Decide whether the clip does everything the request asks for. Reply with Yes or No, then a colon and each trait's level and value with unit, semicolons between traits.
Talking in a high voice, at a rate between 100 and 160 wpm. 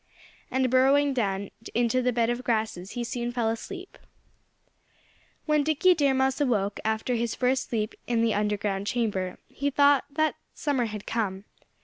Yes: high, 240 Hz; average, 155 wpm